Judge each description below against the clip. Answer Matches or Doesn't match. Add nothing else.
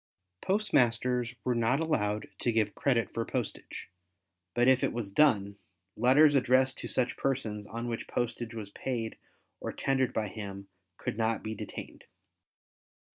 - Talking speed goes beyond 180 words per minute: Doesn't match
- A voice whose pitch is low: Matches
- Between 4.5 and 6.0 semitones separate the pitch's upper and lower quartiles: Doesn't match